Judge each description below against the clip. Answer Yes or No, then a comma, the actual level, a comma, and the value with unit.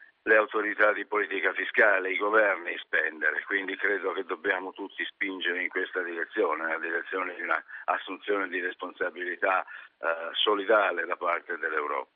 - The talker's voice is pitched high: Yes, very high, 360 Hz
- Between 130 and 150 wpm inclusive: Yes, average, 145 wpm